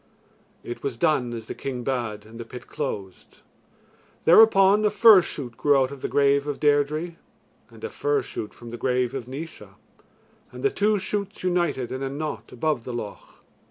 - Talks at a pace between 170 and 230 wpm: Yes, average, 185 wpm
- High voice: No, medium, 140 Hz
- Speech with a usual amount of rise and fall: No, wide, 6.3 semitones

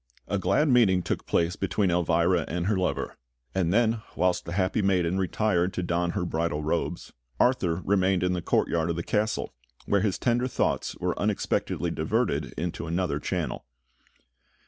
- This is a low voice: Yes, very low, 90 Hz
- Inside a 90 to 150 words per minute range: No, average, 165 wpm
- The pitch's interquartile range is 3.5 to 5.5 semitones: No, average, 2.8 semitones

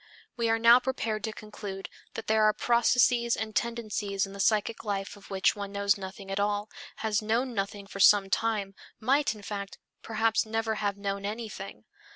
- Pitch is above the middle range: Yes, high, 210 Hz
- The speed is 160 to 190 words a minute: Yes, average, 185 wpm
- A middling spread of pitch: No, narrow, 2.1 semitones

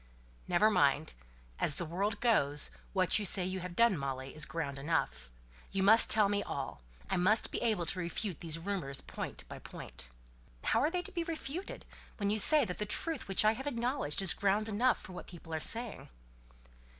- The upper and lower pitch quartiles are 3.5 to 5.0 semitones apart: No, wide, 5.5 semitones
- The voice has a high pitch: Yes, high, 195 Hz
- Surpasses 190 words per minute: Yes, average, 200 wpm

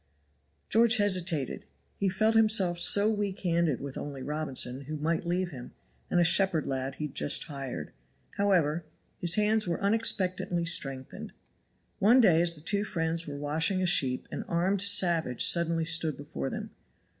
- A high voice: No, medium, 170 Hz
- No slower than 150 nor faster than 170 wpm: Yes, average, 160 wpm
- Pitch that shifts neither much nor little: Yes, average, 4.8 semitones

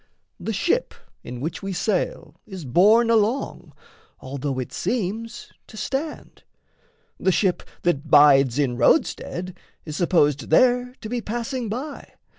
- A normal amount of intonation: No, wide, 8.1 semitones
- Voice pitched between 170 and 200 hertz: Yes, high, 190 Hz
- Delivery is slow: Yes, slow, 130 wpm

